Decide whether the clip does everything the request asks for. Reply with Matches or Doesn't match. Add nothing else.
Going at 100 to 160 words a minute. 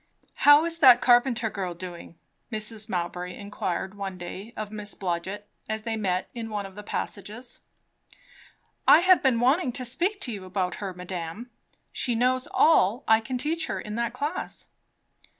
Doesn't match